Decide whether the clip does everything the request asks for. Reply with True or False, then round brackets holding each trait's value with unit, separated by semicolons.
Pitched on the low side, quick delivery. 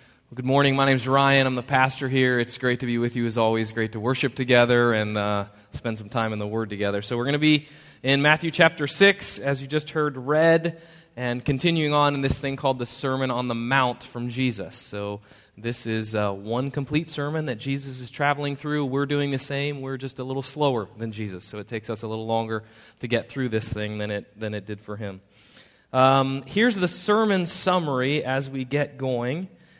True (130 Hz; 220 wpm)